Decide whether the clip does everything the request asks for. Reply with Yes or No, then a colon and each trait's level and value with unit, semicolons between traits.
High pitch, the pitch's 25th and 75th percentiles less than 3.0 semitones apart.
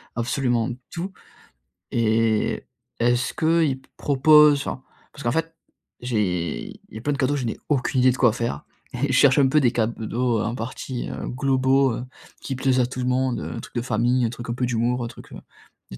No: low, 125 Hz; narrow, 2.5 semitones